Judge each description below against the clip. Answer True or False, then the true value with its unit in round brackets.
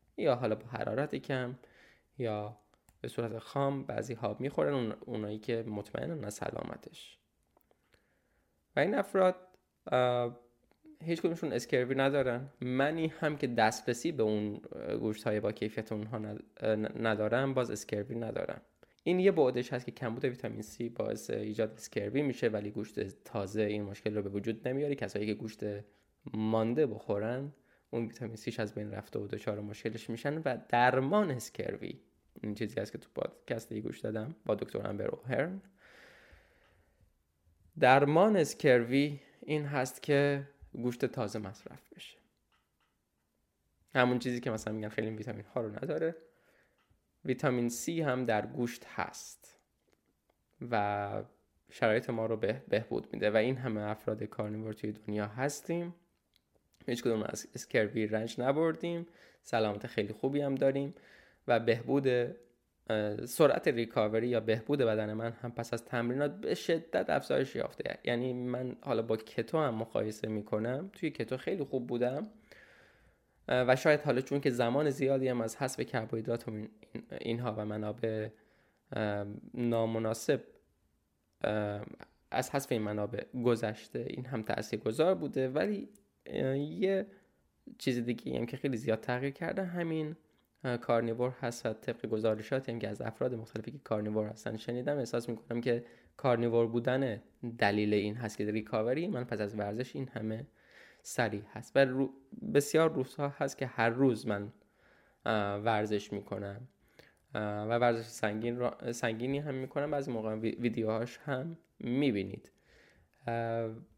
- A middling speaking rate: True (135 wpm)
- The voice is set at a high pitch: False (120 Hz)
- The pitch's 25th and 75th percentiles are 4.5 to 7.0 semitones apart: False (3.7 semitones)